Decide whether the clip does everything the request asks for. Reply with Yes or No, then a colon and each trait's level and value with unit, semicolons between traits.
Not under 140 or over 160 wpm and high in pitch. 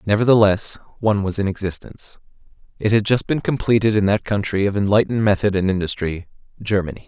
No: average, 155 wpm; low, 105 Hz